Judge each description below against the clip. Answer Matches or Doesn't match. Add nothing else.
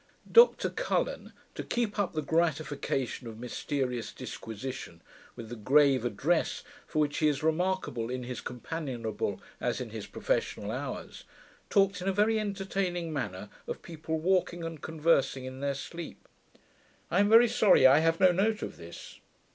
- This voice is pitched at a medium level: Matches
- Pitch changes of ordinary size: Doesn't match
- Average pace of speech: Matches